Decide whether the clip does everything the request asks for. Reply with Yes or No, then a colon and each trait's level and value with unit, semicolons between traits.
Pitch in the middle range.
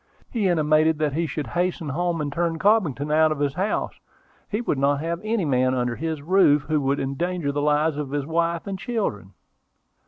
Yes: medium, 155 Hz